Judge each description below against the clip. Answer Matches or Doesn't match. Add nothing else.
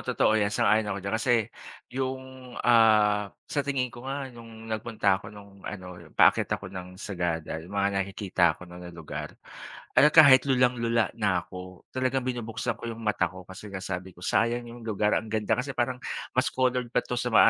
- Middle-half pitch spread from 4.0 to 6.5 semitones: Matches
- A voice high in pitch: Doesn't match